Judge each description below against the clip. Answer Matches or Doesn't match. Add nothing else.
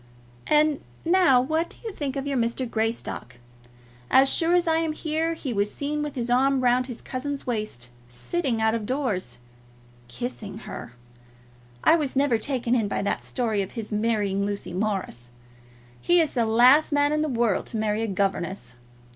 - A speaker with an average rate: Matches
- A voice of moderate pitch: Doesn't match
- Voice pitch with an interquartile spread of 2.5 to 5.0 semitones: Doesn't match